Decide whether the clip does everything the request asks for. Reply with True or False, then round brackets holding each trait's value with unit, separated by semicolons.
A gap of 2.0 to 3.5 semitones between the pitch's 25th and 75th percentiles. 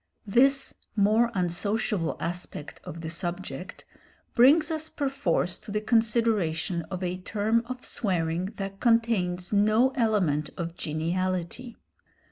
False (4.8 semitones)